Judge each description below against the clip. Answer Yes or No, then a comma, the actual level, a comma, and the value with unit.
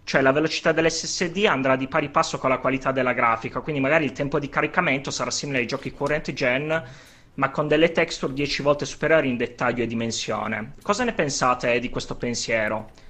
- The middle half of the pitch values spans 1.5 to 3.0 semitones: No, average, 4.3 semitones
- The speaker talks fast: Yes, fast, 195 wpm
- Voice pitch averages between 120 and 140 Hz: Yes, low, 135 Hz